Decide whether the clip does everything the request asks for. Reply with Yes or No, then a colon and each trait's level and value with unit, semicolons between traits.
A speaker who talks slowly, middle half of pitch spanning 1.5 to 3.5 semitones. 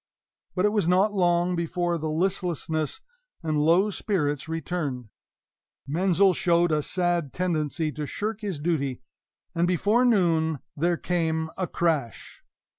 Yes: slow, 130 wpm; average, 2.8 semitones